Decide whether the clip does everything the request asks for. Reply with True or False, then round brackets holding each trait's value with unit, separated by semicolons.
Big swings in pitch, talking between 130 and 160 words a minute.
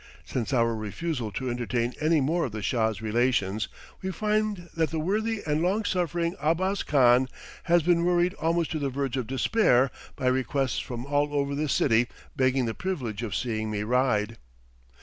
False (6.0 semitones; 175 wpm)